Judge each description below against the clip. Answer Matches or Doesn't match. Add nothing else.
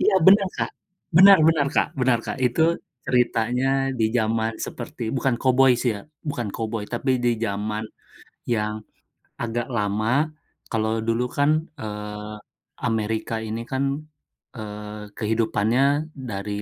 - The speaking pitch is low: Matches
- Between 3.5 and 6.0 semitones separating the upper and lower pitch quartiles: Doesn't match